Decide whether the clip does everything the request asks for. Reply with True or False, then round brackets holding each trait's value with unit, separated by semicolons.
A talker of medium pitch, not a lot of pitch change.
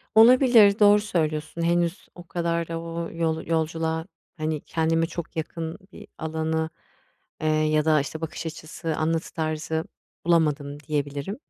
True (160 Hz; 1.4 semitones)